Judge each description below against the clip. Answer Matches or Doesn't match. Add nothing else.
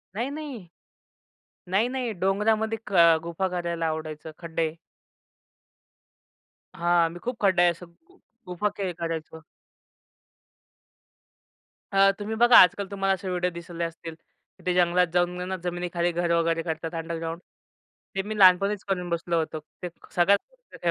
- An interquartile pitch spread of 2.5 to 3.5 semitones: Matches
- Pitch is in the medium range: Matches